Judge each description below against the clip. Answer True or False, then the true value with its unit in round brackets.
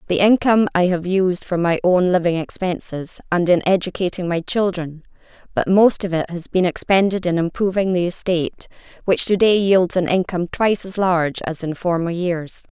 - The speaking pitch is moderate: True (180 Hz)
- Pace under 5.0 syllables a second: False (5.2 syllables/s)